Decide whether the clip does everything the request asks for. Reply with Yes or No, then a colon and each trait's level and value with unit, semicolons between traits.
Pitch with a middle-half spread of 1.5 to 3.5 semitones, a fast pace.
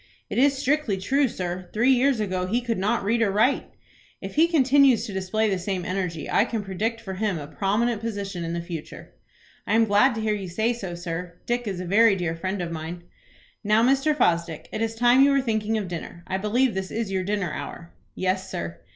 No: average, 4.4 semitones; fast, 220 wpm